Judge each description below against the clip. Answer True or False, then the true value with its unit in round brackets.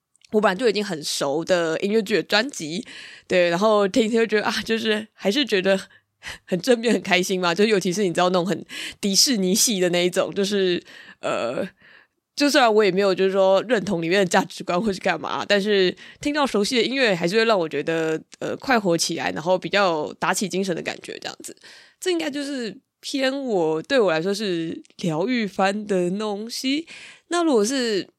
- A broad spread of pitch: False (3.8 semitones)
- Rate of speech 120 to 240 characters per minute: False (295 characters per minute)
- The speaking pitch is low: False (200 Hz)